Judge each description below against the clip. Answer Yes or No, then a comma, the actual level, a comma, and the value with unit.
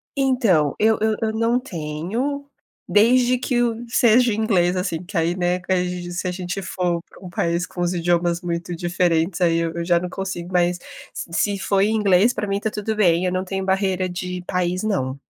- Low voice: No, medium, 185 Hz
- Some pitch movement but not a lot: Yes, average, 3.6 semitones